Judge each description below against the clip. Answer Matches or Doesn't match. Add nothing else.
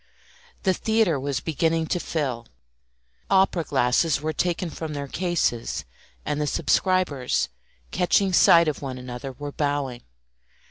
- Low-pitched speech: Doesn't match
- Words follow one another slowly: Matches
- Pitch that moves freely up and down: Doesn't match